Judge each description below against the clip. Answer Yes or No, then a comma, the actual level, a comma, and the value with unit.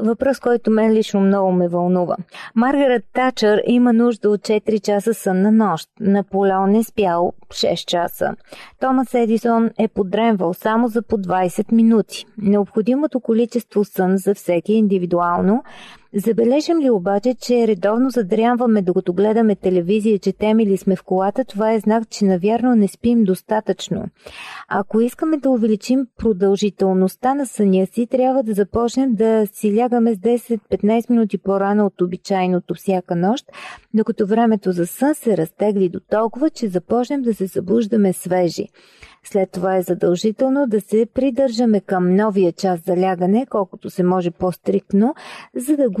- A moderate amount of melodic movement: Yes, average, 3.5 semitones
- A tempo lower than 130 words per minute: No, average, 150 wpm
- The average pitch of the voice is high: Yes, high, 215 Hz